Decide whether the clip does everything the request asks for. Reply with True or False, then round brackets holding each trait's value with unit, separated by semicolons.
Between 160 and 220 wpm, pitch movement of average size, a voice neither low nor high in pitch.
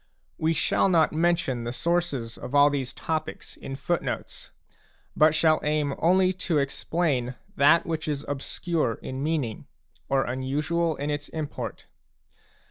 False (135 wpm; 3.4 semitones; 150 Hz)